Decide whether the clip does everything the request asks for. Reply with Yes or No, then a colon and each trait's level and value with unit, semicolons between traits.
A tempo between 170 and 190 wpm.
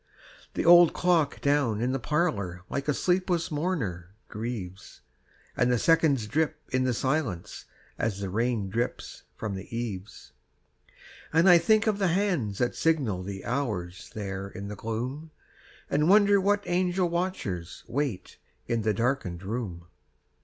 No: average, 145 wpm